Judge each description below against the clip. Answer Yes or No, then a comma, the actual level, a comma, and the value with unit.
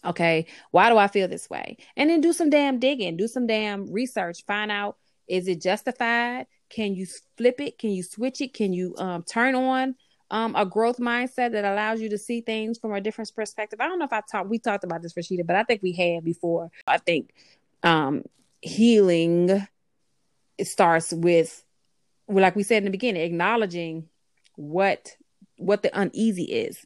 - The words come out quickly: No, average, 190 wpm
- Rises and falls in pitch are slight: No, average, 4.3 semitones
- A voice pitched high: Yes, high, 210 Hz